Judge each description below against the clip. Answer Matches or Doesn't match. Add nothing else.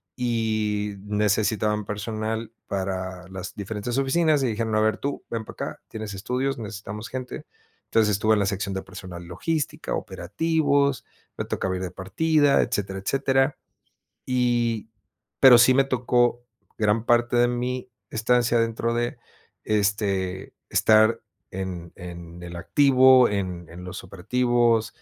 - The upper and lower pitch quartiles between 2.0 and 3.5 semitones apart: Doesn't match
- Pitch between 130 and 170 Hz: Doesn't match